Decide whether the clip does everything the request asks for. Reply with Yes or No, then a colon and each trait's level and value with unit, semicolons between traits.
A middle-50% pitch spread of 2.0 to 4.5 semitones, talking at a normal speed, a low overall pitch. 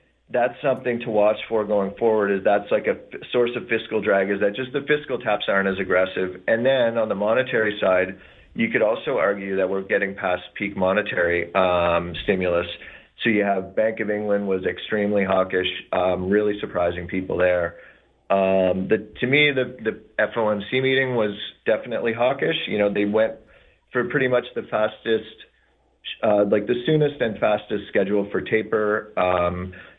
Yes: average, 2.8 semitones; average, 175 wpm; low, 105 Hz